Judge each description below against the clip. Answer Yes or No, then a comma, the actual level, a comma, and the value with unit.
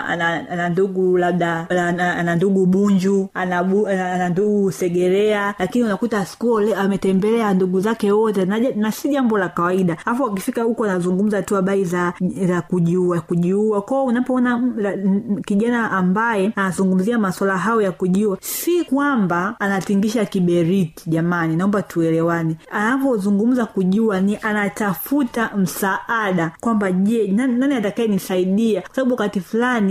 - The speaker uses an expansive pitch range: No, average, 3.2 semitones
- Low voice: No, high, 195 Hz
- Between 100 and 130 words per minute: Yes, average, 110 wpm